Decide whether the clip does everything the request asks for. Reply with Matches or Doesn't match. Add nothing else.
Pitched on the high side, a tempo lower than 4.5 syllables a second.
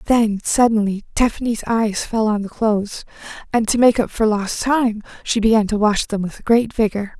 Doesn't match